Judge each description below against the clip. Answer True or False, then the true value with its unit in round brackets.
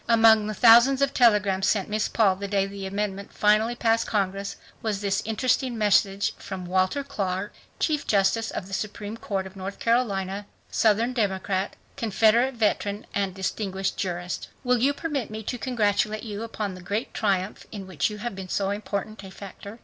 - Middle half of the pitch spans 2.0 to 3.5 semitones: True (2.7 semitones)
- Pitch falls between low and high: False (205 Hz)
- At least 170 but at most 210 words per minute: True (175 wpm)